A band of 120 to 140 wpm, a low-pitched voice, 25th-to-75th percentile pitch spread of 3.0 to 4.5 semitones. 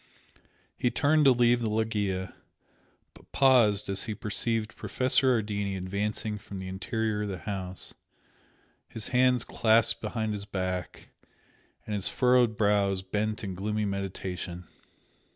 No: slow, 135 wpm; low, 105 Hz; narrow, 2.6 semitones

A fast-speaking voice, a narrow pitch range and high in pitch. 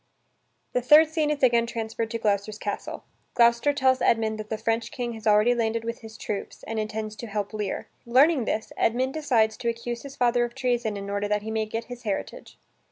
Yes: fast, 210 wpm; narrow, 2.2 semitones; high, 230 Hz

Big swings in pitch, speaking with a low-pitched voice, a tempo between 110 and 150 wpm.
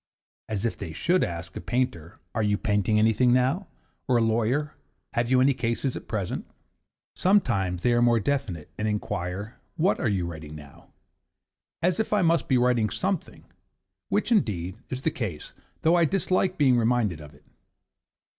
No: wide, 6.5 semitones; low, 115 Hz; average, 170 wpm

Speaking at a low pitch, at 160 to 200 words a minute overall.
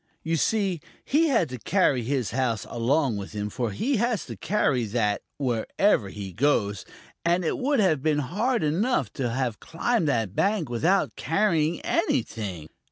No: medium, 145 Hz; average, 165 wpm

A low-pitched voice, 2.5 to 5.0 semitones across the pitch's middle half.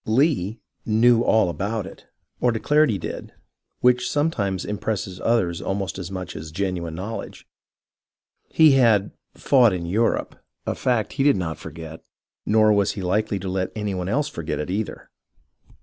Yes: low, 100 Hz; average, 4.2 semitones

